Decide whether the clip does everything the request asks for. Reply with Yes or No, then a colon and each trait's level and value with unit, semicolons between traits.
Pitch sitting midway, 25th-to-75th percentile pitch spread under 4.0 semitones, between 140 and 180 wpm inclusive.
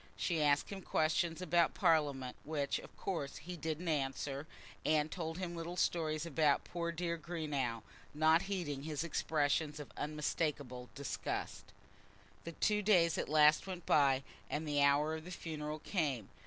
Yes: medium, 155 Hz; narrow, 2.6 semitones; average, 155 wpm